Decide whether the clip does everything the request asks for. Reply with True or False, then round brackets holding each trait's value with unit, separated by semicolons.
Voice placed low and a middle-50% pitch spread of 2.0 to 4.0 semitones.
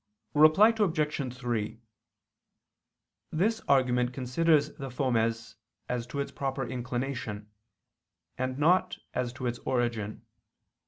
True (130 Hz; 3.4 semitones)